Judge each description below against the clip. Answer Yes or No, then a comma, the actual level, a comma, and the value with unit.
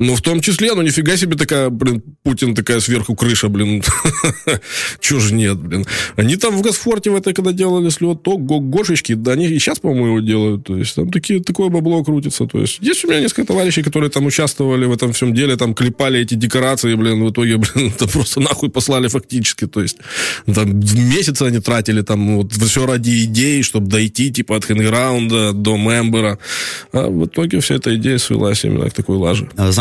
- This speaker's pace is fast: Yes, fast, 200 wpm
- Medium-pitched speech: No, low, 125 Hz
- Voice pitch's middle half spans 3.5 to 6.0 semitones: Yes, average, 5.2 semitones